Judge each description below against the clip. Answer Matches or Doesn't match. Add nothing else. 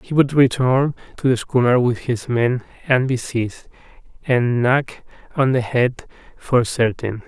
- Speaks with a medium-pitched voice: Doesn't match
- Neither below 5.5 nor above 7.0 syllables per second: Doesn't match